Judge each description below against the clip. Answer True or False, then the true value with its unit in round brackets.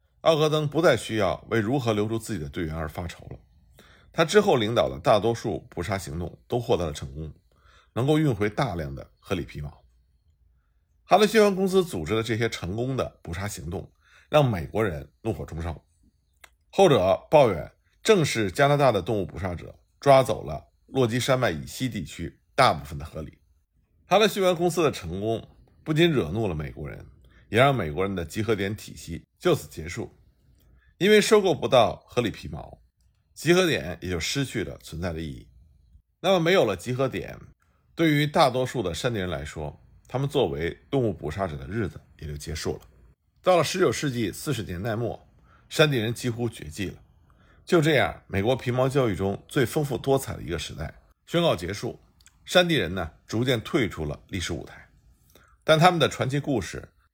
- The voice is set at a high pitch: False (105 Hz)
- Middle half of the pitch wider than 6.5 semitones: True (9.0 semitones)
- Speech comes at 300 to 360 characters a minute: False (275 characters per minute)